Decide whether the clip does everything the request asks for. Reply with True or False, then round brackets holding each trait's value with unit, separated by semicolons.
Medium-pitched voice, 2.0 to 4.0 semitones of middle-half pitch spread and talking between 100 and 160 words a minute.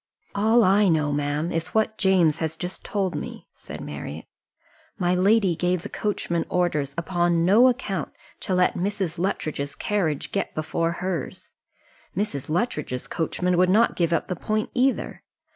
True (180 Hz; 3.7 semitones; 155 wpm)